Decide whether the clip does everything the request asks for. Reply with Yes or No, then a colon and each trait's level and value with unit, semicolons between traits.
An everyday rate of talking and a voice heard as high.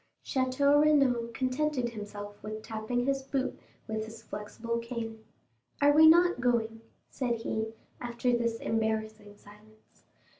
No: slow, 125 wpm; high, 235 Hz